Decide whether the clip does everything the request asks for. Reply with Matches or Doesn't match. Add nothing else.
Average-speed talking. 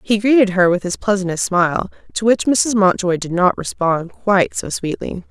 Matches